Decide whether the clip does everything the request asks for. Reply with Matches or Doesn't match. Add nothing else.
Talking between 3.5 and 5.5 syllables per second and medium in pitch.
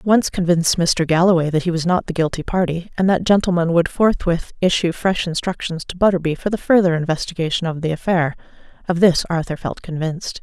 Doesn't match